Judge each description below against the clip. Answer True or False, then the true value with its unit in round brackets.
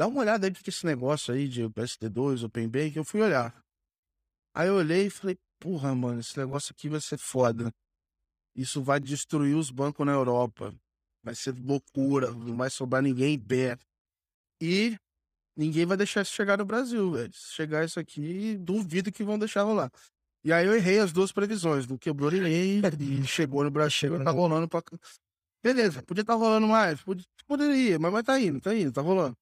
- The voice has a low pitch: False (150 Hz)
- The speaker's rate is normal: False (190 wpm)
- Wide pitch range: True (7.1 semitones)